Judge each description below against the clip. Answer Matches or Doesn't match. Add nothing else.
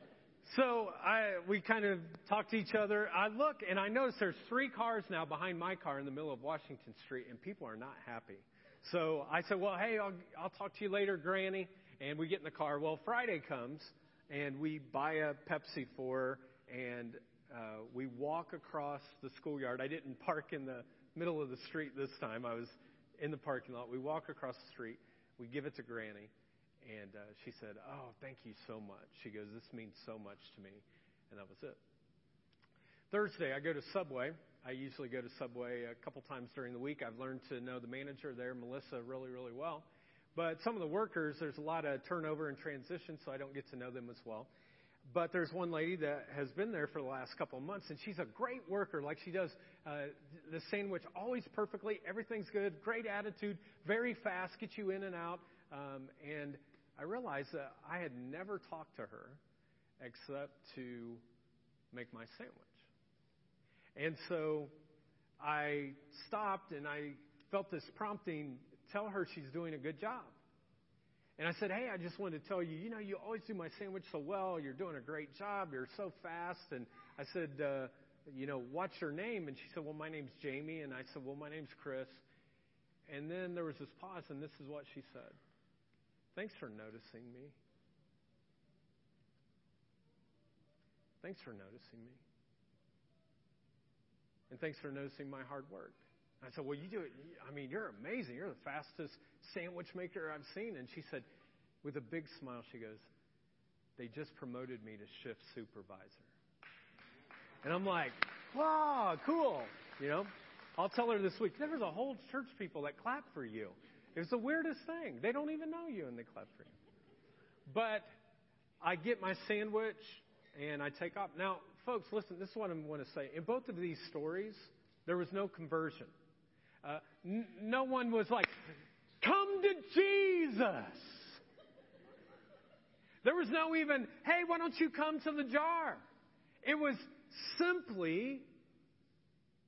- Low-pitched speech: Doesn't match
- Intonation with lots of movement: Matches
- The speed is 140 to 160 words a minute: Doesn't match